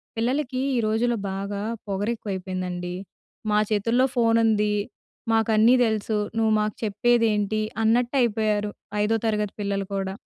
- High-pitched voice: Yes, high, 215 Hz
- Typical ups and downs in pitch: No, narrow, 2.2 semitones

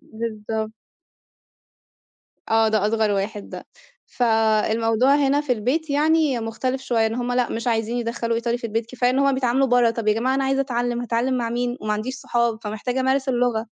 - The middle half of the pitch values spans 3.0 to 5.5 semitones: No, narrow, 2.6 semitones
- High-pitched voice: Yes, high, 235 Hz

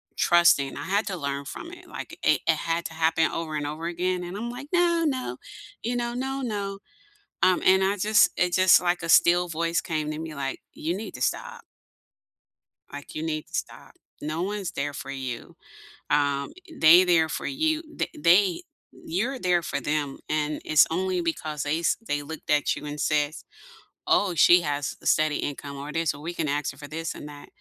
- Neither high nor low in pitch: Yes, medium, 165 Hz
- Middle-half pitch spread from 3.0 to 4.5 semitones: Yes, average, 4.1 semitones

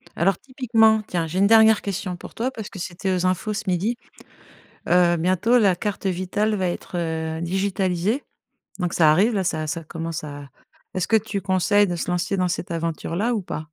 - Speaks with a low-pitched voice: No, medium, 185 Hz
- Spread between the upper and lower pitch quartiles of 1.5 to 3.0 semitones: No, average, 3.4 semitones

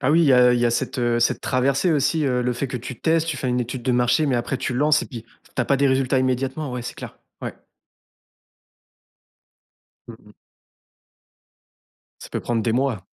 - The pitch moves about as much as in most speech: No, narrow, 2.2 semitones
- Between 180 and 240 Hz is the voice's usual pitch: No, low, 130 Hz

